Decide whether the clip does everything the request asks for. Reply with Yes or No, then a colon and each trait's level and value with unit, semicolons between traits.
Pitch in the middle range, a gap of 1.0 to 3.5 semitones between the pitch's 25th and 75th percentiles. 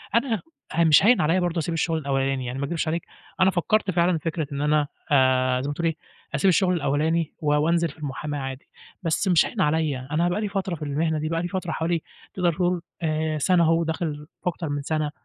Yes: medium, 160 Hz; average, 2.9 semitones